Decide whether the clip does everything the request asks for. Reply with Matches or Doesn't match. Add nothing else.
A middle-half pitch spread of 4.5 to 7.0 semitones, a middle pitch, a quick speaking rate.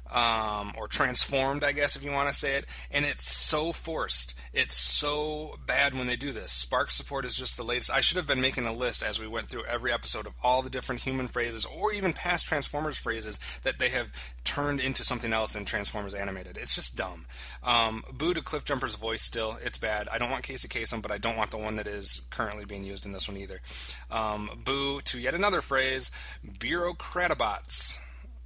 Doesn't match